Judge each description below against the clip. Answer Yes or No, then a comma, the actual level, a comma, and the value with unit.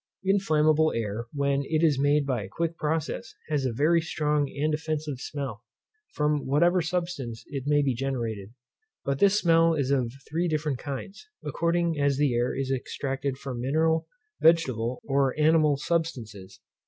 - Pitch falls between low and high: Yes, medium, 145 Hz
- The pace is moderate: Yes, average, 155 wpm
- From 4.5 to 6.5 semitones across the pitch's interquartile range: No, average, 3.4 semitones